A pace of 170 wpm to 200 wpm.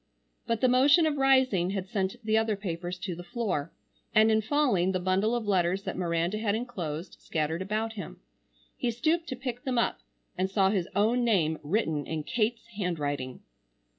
Yes: average, 180 wpm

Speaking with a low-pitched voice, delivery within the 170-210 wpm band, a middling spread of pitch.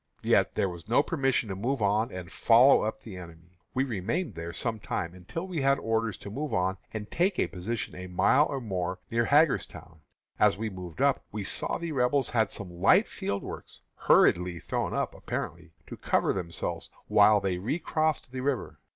No: low, 110 Hz; average, 195 wpm; wide, 6.7 semitones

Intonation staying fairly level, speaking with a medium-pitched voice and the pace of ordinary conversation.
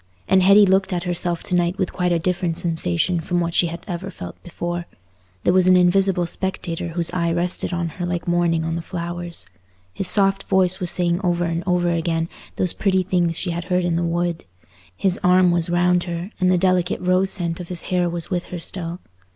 No: narrow, 1.3 semitones; medium, 175 Hz; fast, 215 wpm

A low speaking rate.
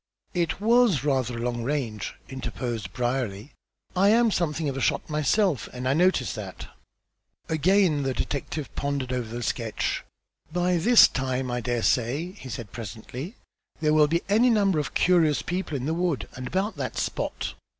No: average, 170 wpm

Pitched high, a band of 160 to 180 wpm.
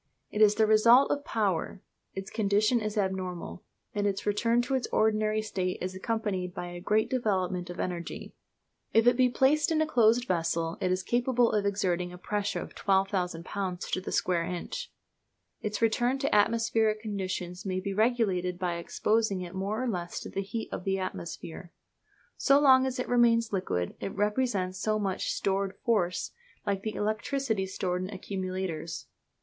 Yes: high, 205 Hz; average, 175 wpm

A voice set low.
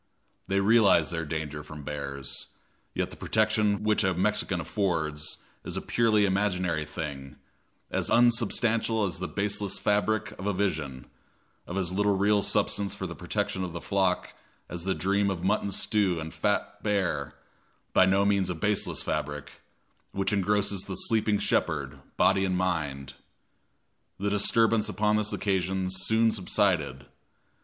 Yes: very low, 95 Hz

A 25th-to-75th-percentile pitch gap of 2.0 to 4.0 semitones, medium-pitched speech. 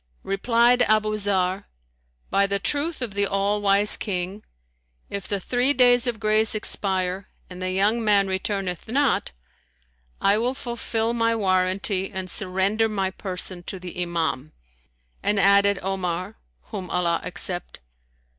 No: average, 2.8 semitones; high, 200 Hz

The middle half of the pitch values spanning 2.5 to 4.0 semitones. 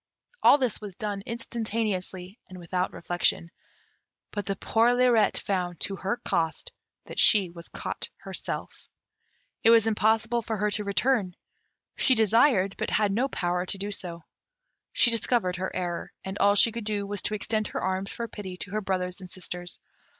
Yes: average, 3.4 semitones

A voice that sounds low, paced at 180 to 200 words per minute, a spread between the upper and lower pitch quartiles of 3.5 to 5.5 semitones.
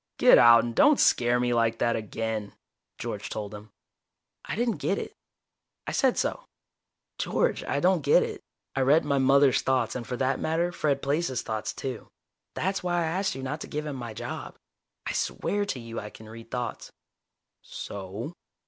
Yes: low, 130 Hz; average, 185 wpm; average, 5.0 semitones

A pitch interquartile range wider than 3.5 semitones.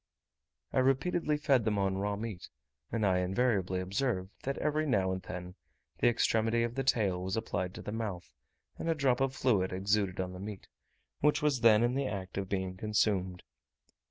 Yes: average, 5.3 semitones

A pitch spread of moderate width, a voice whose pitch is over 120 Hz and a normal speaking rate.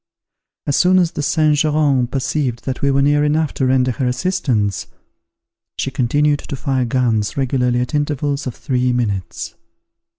Yes: average, 3.0 semitones; low, 135 Hz; average, 160 wpm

